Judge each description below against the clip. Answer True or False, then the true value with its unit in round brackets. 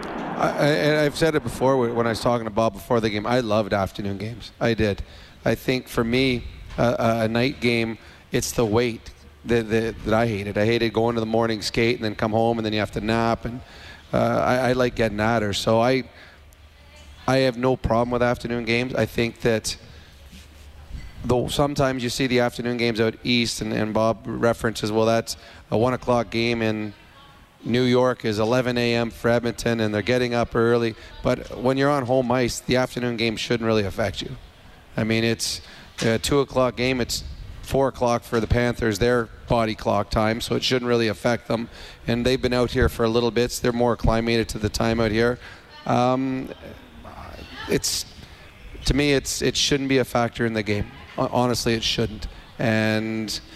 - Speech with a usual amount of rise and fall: False (2.2 semitones)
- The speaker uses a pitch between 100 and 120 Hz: True (115 Hz)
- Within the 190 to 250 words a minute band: True (200 wpm)